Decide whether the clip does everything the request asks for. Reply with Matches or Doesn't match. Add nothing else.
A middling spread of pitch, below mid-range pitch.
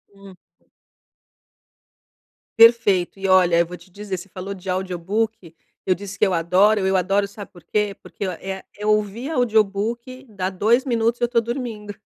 Doesn't match